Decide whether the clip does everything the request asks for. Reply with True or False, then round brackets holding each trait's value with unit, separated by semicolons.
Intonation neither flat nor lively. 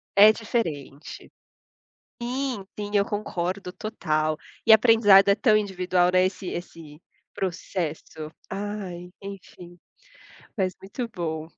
True (3.4 semitones)